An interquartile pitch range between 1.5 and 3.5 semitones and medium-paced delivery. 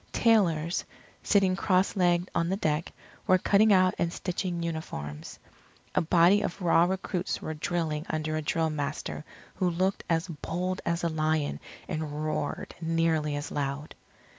Yes: average, 2.9 semitones; average, 150 wpm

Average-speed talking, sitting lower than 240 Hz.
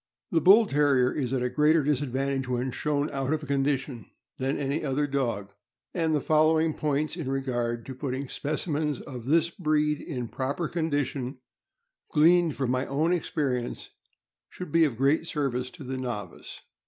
Yes: average, 160 wpm; medium, 140 Hz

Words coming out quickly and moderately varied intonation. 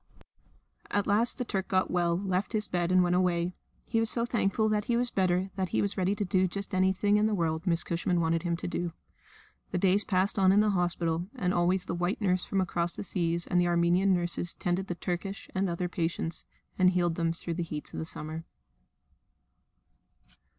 No: fast, 215 wpm; narrow, 2.2 semitones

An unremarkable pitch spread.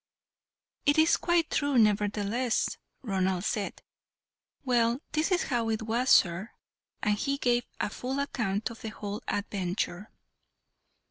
Yes: average, 4.1 semitones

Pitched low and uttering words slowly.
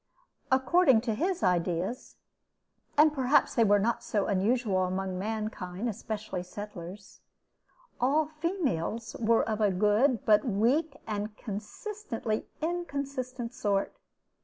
No: high, 225 Hz; slow, 110 wpm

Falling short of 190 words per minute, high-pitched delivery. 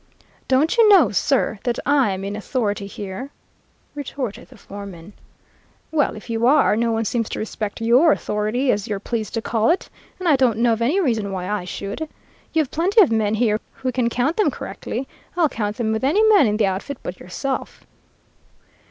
No: average, 195 wpm; high, 230 Hz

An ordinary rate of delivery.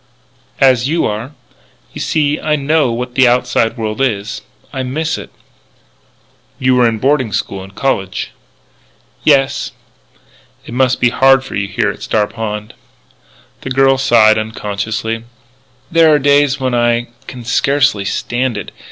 Yes: average, 145 wpm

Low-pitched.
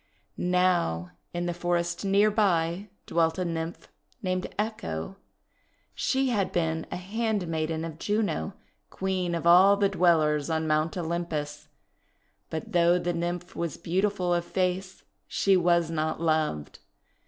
No: medium, 175 Hz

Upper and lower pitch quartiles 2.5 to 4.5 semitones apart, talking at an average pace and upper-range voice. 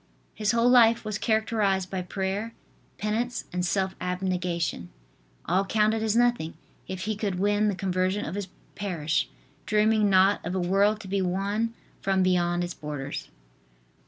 Yes: average, 2.8 semitones; average, 155 wpm; high, 195 Hz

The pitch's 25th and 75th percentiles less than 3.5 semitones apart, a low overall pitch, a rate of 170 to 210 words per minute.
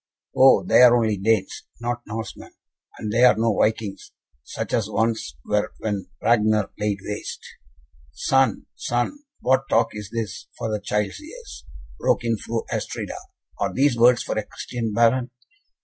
No: narrow, 2.5 semitones; low, 115 Hz; average, 160 wpm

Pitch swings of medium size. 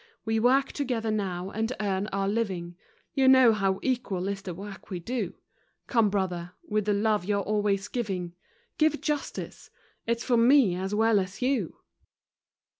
Yes: average, 3.5 semitones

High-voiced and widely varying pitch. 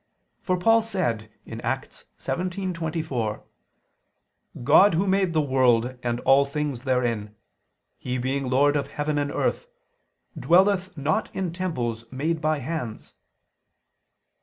No: medium, 145 Hz; wide, 5.7 semitones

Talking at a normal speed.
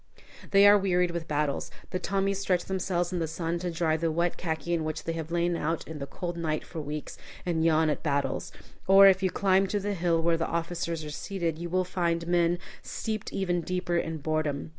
No: fast, 220 wpm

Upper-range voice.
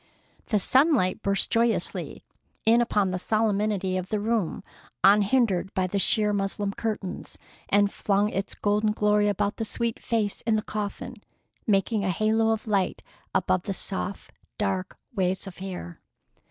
Yes: high, 205 Hz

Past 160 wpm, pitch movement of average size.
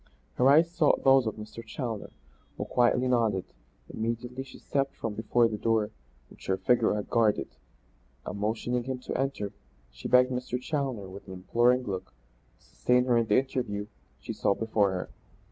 Yes: average, 175 wpm; average, 3.4 semitones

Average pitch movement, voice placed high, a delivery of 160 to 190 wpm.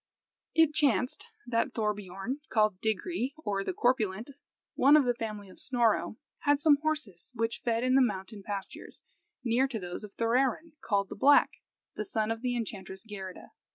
Yes: average, 4.5 semitones; high, 230 Hz; average, 165 wpm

